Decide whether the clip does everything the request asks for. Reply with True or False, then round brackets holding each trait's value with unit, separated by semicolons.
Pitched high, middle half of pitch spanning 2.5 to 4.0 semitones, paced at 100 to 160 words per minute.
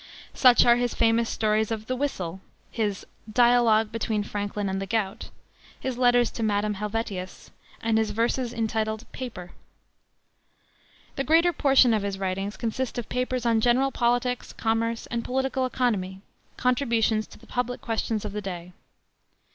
True (225 Hz; 2.8 semitones; 150 wpm)